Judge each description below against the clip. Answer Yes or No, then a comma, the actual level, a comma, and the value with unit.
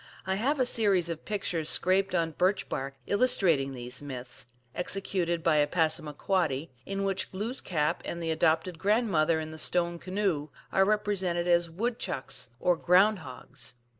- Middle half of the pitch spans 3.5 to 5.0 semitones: Yes, average, 4.1 semitones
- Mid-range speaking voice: Yes, medium, 175 Hz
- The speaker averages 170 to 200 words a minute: No, average, 155 wpm